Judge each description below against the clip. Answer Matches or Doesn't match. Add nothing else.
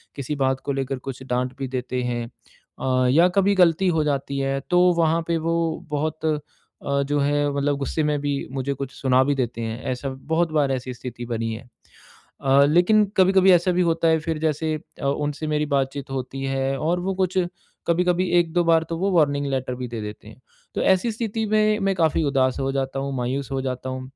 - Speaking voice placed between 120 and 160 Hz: Matches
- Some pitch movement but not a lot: Matches